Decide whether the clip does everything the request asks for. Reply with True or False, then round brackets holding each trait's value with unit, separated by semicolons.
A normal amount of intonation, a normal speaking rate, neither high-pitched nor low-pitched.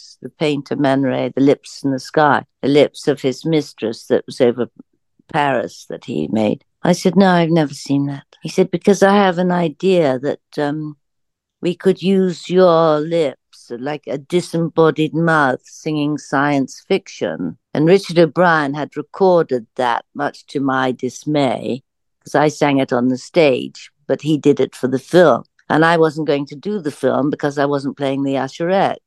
True (3.7 semitones; 180 wpm; 150 Hz)